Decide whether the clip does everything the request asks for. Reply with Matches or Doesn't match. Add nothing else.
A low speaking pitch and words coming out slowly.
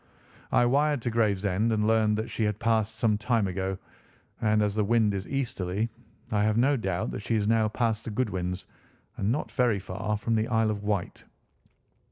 Doesn't match